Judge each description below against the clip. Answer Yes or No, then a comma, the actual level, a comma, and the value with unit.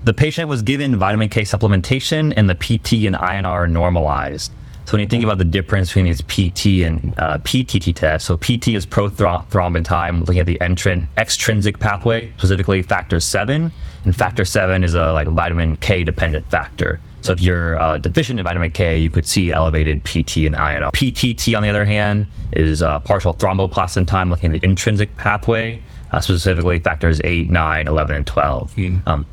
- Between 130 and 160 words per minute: No, average, 185 wpm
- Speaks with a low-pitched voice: Yes, very low, 95 Hz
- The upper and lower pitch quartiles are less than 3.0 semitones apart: No, average, 4.3 semitones